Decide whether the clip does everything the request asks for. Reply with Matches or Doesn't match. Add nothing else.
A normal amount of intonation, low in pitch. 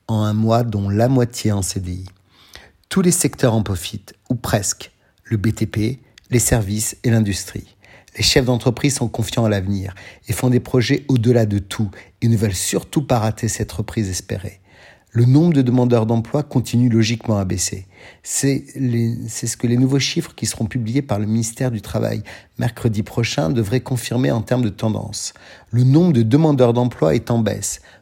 Matches